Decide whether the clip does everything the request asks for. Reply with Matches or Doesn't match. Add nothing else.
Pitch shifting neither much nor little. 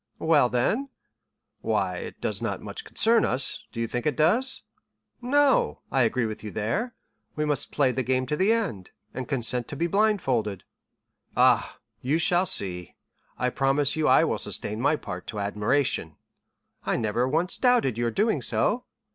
Doesn't match